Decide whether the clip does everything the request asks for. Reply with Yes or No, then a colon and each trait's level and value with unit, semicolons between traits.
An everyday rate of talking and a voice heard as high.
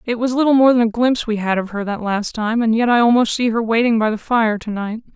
No: fast, 305 wpm; high, 225 Hz